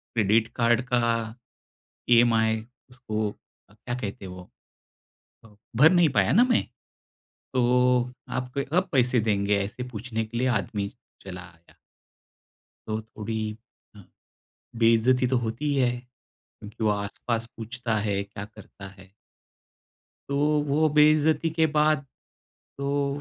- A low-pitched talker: Yes, low, 120 Hz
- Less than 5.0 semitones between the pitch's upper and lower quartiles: Yes, average, 3.6 semitones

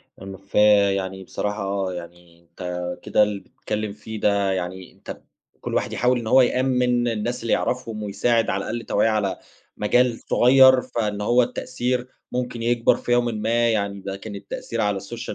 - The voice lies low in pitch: Yes, low, 110 Hz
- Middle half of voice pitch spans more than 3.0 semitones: Yes, average, 3.6 semitones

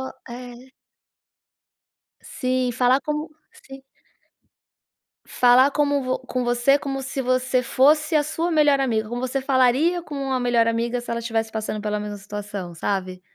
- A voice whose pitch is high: Yes, very high, 255 Hz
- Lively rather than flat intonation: No, average, 3.1 semitones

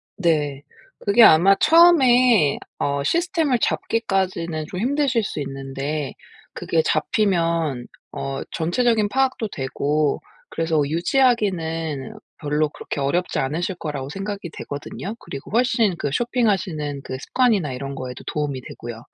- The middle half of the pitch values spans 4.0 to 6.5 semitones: No, wide, 7.6 semitones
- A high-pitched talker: No, medium, 165 Hz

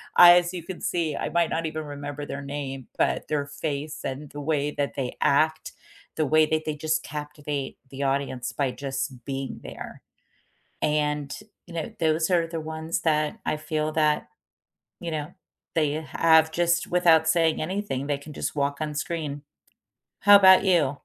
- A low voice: No, medium, 155 Hz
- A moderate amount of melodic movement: No, narrow, 2.1 semitones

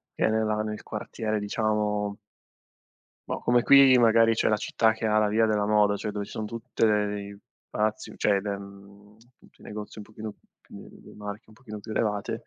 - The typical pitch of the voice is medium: No, low, 105 Hz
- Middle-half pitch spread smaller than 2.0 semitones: Yes, narrow, 1.1 semitones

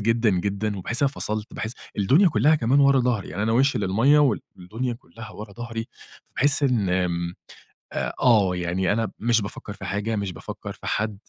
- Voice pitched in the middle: No, low, 110 Hz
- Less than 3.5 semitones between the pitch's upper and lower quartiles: No, average, 3.8 semitones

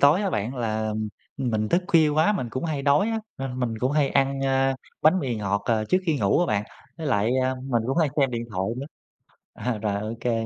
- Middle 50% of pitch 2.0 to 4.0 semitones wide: No, average, 4.8 semitones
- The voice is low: Yes, low, 130 Hz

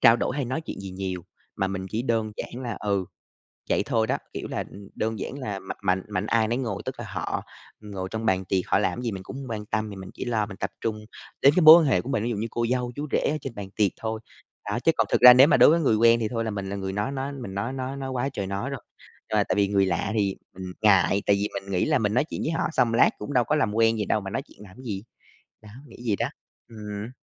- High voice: No, low, 110 Hz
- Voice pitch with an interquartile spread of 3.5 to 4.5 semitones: Yes, average, 3.9 semitones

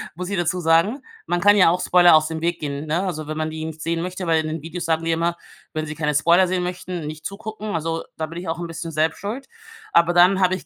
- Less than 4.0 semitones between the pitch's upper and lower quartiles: Yes, narrow, 2.4 semitones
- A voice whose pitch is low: No, medium, 170 Hz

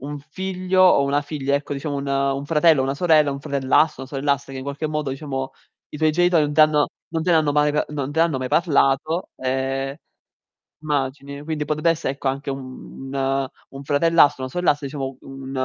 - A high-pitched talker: No, medium, 145 Hz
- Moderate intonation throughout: No, narrow, 2.3 semitones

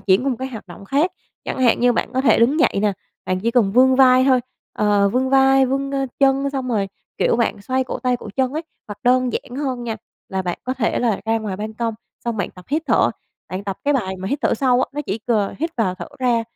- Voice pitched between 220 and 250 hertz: Yes, high, 245 Hz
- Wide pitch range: No, average, 4.1 semitones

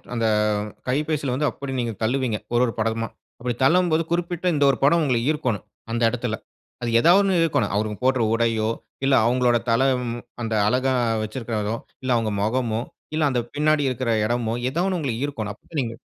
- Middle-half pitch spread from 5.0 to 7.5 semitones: No, average, 4.1 semitones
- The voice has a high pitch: No, low, 125 Hz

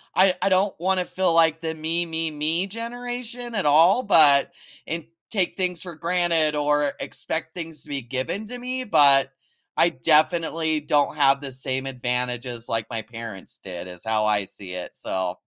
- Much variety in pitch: Yes, wide, 5.7 semitones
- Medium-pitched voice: Yes, medium, 155 Hz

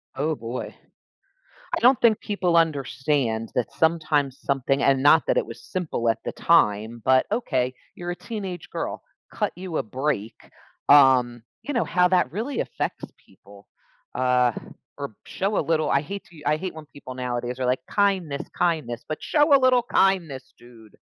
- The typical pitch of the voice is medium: Yes, medium, 150 Hz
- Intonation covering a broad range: Yes, wide, 6.1 semitones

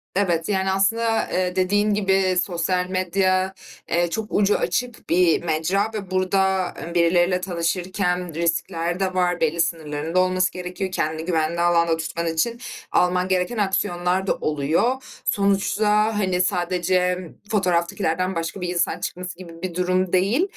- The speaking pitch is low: No, medium, 185 Hz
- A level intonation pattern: Yes, narrow, 2.0 semitones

